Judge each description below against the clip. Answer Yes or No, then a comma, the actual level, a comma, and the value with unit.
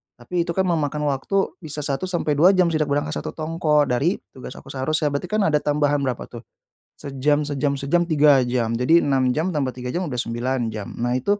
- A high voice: No, medium, 145 Hz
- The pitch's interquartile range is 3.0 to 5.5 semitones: Yes, average, 3.8 semitones